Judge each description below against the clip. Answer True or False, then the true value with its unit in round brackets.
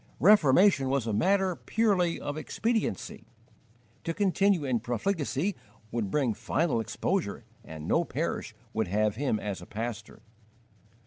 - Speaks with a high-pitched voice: False (140 Hz)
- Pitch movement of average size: False (8.9 semitones)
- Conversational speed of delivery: False (130 wpm)